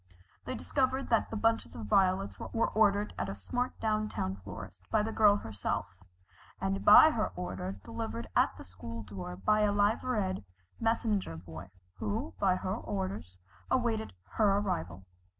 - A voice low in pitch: Yes, low, 115 Hz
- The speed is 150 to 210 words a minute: Yes, average, 155 wpm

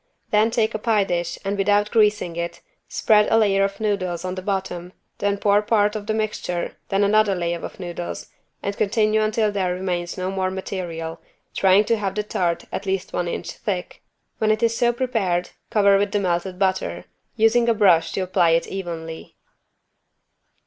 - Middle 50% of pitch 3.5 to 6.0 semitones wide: No, average, 3.0 semitones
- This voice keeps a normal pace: Yes, average, 185 wpm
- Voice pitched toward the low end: No, high, 195 Hz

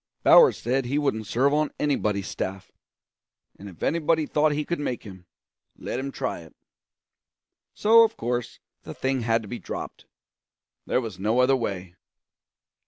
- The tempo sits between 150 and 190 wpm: Yes, average, 160 wpm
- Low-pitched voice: Yes, low, 125 Hz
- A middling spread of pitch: No, wide, 5.7 semitones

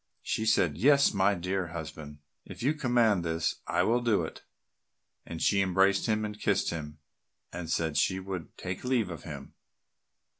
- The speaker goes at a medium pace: Yes, average, 165 wpm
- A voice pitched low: Yes, very low, 95 Hz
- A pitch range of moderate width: Yes, average, 4.5 semitones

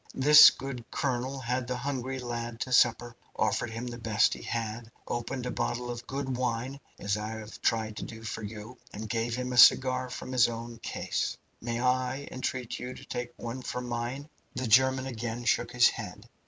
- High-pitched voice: No, low, 120 Hz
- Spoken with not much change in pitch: Yes, narrow, 1.9 semitones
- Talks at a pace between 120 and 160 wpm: No, average, 195 wpm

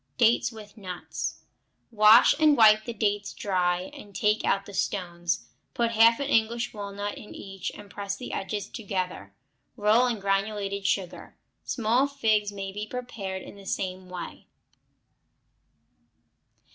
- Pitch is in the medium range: No, high, 205 Hz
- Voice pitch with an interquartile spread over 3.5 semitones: No, narrow, 2.4 semitones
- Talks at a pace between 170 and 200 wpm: No, average, 140 wpm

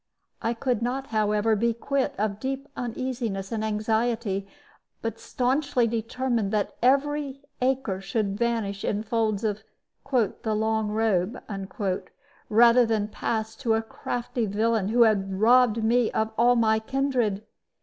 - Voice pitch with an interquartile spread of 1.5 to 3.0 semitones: Yes, narrow, 2.4 semitones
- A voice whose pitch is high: Yes, high, 225 Hz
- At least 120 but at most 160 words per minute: Yes, slow, 135 wpm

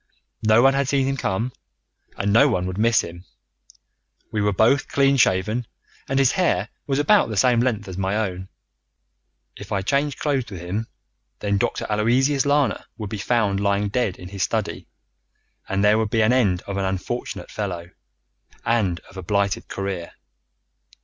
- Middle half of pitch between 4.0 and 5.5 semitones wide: Yes, average, 4.7 semitones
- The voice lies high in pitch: No, low, 105 Hz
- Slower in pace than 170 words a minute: No, average, 175 wpm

